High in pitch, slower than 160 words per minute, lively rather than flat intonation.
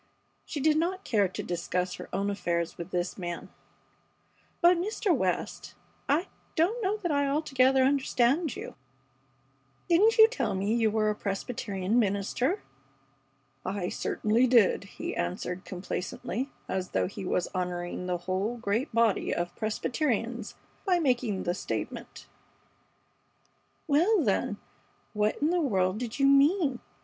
Yes: high, 230 Hz; average, 140 wpm; wide, 7.8 semitones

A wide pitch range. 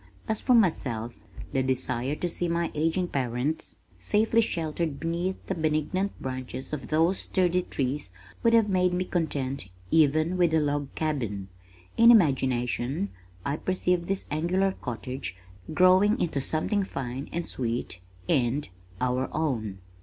Yes: wide, 5.7 semitones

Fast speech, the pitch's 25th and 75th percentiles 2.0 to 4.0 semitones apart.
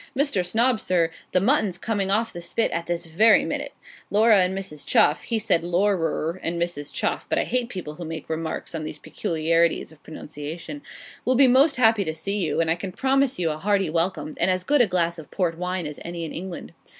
No: fast, 220 wpm; average, 4.4 semitones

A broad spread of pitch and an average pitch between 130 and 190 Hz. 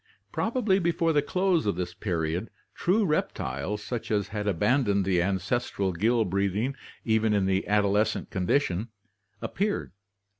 No: wide, 6.6 semitones; low, 105 Hz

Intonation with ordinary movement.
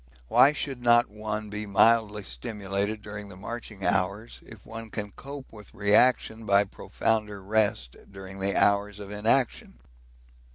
No: narrow, 2.0 semitones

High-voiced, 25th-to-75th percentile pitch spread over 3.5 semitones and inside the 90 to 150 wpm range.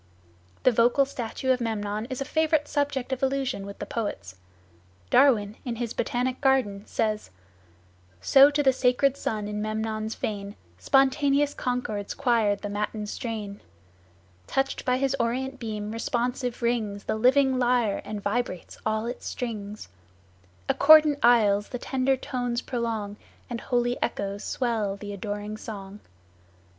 Yes: high, 235 Hz; average, 3.9 semitones; average, 140 wpm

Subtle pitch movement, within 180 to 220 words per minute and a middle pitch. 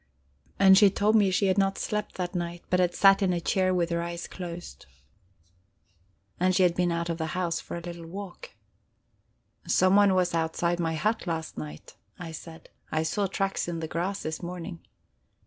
Yes: narrow, 2.3 semitones; average, 190 wpm; medium, 175 Hz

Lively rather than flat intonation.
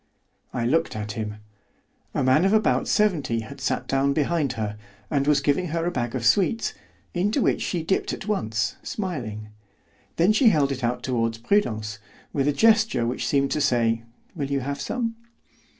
Yes: wide, 7.0 semitones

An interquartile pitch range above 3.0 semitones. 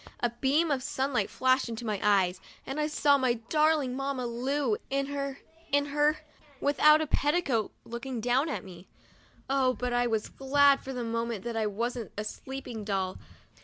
Yes: average, 3.5 semitones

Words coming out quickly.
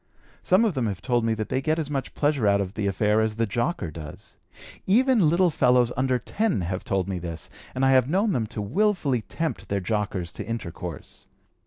Yes: fast, 210 wpm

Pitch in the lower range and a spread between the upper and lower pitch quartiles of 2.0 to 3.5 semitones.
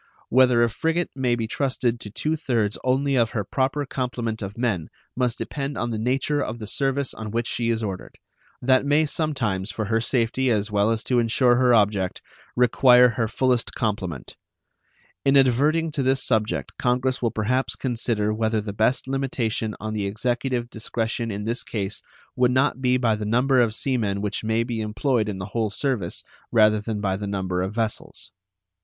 Yes: low, 115 Hz; average, 3.2 semitones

